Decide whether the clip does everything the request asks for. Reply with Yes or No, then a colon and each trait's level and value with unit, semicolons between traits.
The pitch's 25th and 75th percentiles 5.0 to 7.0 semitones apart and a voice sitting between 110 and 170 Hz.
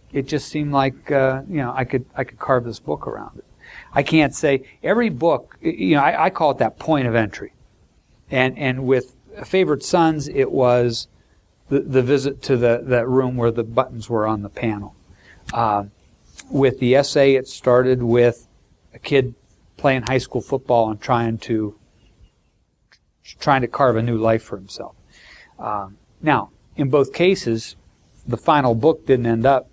No: average, 3.4 semitones; low, 125 Hz